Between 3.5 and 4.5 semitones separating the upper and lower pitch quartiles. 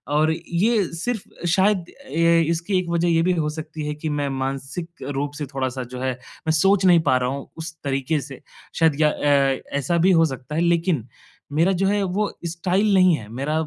Yes: average, 4.2 semitones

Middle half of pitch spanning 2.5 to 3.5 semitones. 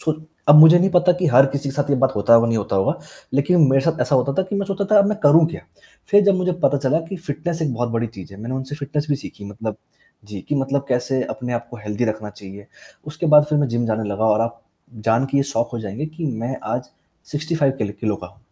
No: average, 5.3 semitones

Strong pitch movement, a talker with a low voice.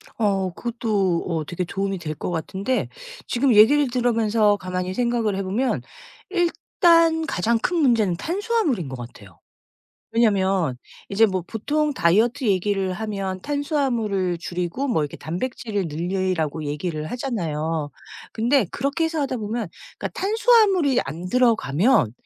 No: wide, 6.3 semitones; high, 210 Hz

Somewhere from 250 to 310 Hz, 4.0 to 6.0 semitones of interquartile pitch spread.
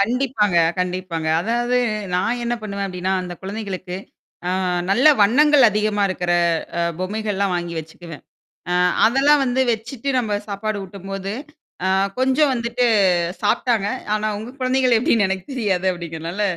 No: high, 210 Hz; average, 4.6 semitones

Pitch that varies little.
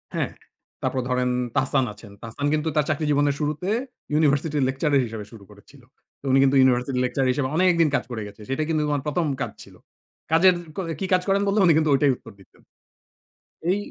No: average, 3.6 semitones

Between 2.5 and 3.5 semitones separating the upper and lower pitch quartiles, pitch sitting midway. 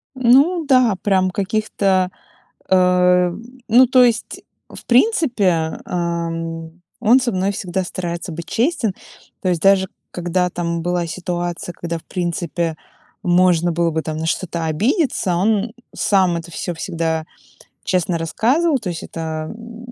No: average, 4.3 semitones; medium, 180 Hz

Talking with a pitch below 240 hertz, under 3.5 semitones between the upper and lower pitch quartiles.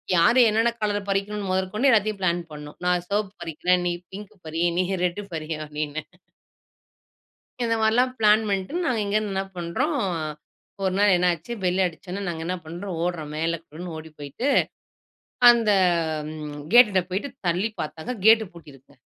No: medium, 185 Hz; average, 4.3 semitones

